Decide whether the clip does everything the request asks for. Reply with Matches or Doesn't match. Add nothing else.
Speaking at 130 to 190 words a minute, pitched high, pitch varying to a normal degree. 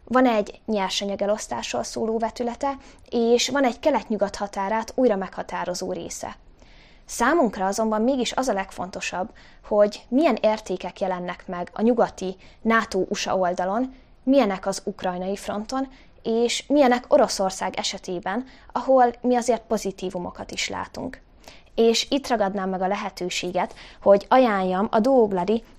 Doesn't match